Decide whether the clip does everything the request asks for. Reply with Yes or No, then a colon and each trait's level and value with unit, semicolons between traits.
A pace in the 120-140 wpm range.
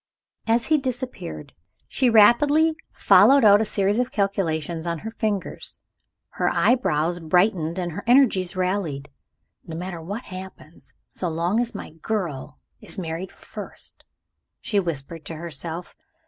Yes: slow, 135 wpm